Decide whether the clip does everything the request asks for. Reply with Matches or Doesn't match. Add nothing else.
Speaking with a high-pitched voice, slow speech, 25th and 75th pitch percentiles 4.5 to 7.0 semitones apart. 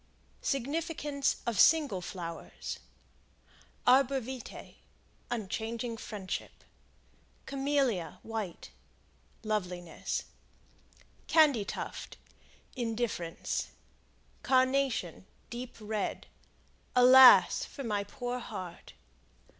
Matches